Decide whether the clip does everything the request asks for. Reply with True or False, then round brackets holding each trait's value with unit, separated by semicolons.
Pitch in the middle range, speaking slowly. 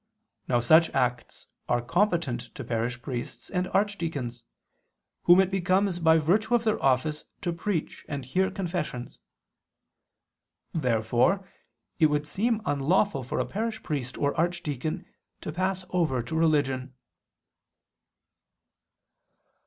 True (160 Hz; 120 wpm)